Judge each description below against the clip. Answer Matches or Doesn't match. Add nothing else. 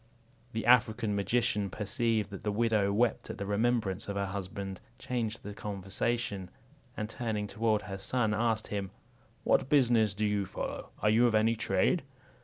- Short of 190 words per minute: Matches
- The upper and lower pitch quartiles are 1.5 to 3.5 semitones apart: Matches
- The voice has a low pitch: Matches